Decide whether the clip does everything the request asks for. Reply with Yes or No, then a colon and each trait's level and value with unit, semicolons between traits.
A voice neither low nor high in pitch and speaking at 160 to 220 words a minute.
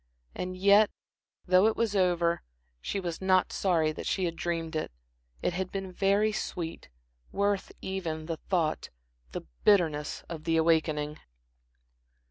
No: medium, 180 Hz; average, 140 wpm